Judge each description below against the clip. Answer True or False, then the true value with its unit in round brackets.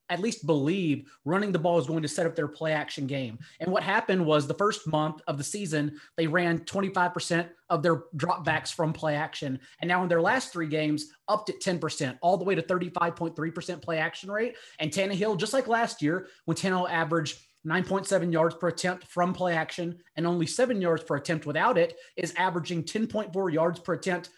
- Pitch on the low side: False (170 Hz)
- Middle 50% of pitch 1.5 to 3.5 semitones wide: True (2.9 semitones)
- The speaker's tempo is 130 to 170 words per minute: False (200 wpm)